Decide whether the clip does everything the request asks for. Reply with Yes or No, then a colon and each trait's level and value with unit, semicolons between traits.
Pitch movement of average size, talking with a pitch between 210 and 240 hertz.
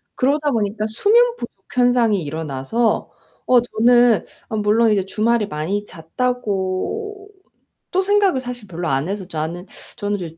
Yes: average, 4.9 semitones; high, 220 Hz